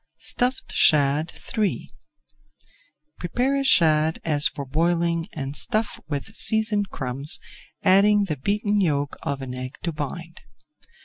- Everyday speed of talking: No, slow, 125 wpm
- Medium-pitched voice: Yes, medium, 165 Hz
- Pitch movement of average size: No, wide, 6.1 semitones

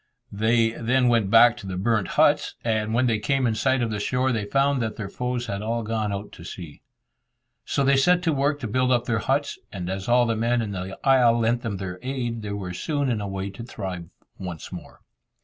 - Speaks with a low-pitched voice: Yes, low, 115 Hz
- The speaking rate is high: Yes, fast, 235 wpm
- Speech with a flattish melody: No, average, 3.8 semitones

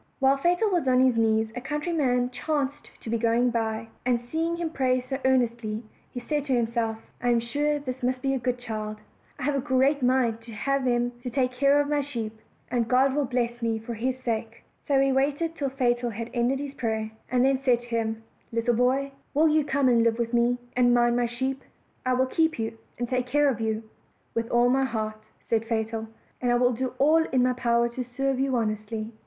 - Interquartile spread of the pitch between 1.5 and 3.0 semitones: Yes, average, 2.7 semitones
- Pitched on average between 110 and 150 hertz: No, very high, 250 Hz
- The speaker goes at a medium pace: No, fast, 220 wpm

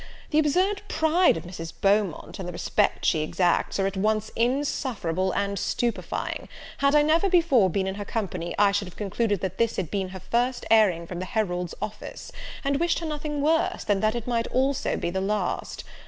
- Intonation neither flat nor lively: No, wide, 6.6 semitones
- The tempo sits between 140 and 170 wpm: No, average, 200 wpm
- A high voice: Yes, high, 210 Hz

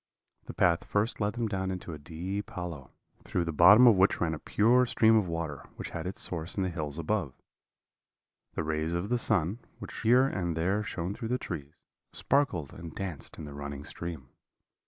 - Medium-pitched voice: No, very low, 90 Hz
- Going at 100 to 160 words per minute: No, average, 200 wpm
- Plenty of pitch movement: No, average, 4.5 semitones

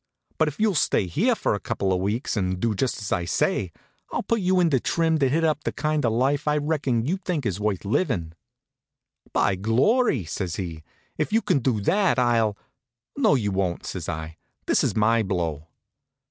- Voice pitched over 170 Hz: No, low, 120 Hz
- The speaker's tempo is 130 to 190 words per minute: No, average, 200 wpm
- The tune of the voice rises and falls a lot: Yes, wide, 8.1 semitones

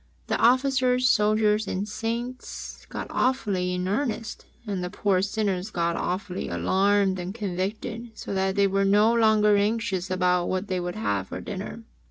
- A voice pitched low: No, high, 200 Hz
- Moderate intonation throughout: Yes, average, 3.0 semitones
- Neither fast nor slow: Yes, average, 160 wpm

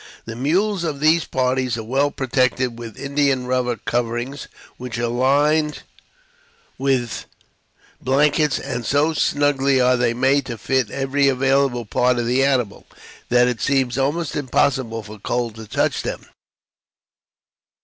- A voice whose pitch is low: Yes, low, 130 Hz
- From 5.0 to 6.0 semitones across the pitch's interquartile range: No, narrow, 2.6 semitones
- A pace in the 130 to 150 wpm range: Yes, average, 140 wpm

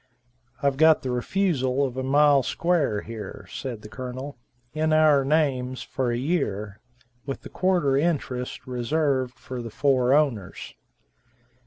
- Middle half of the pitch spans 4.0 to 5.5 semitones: No, average, 3.2 semitones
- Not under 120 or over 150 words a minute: Yes, average, 140 wpm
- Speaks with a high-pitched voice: No, low, 135 Hz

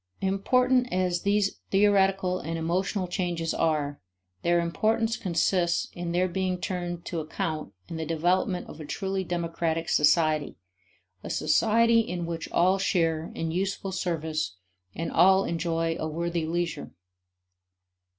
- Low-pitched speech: No, medium, 175 Hz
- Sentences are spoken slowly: Yes, slow, 130 wpm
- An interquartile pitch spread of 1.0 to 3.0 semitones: Yes, average, 2.7 semitones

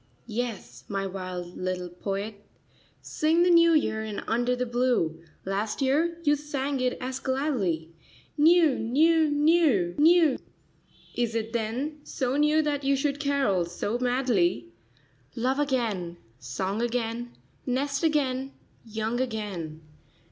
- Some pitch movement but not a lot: No, wide, 6.5 semitones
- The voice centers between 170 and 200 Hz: No, high, 245 Hz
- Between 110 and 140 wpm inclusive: Yes, slow, 135 wpm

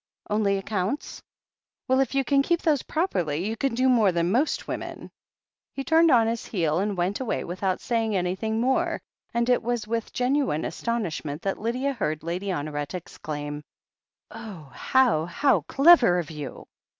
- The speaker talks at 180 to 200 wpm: No, average, 165 wpm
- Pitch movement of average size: No, wide, 6.7 semitones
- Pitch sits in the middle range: No, high, 215 Hz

